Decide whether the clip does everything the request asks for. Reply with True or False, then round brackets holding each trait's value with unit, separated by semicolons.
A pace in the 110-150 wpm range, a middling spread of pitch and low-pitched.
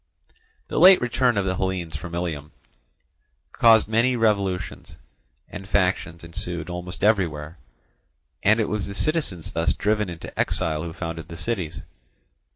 True (140 wpm; 4.3 semitones; 90 Hz)